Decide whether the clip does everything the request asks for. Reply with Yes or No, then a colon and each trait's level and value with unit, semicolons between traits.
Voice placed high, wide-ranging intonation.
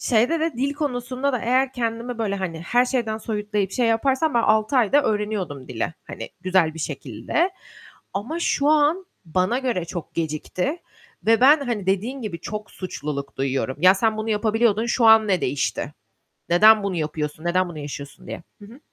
Yes: high, 215 Hz; wide, 6.0 semitones